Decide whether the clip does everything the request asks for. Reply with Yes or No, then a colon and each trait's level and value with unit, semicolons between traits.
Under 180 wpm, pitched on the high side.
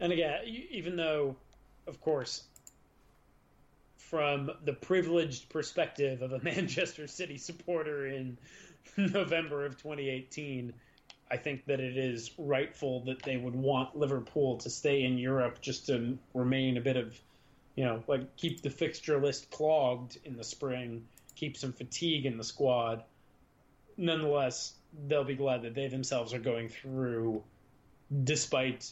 No: average, 140 wpm; low, 135 Hz